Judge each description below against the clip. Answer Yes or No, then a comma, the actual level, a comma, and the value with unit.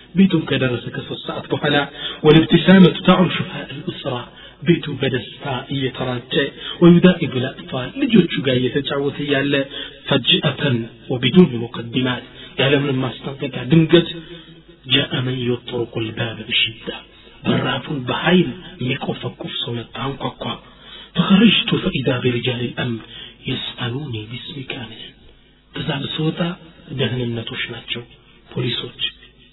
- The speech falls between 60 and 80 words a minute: No, average, 100 wpm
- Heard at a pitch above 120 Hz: Yes, medium, 140 Hz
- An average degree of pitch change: Yes, average, 4.6 semitones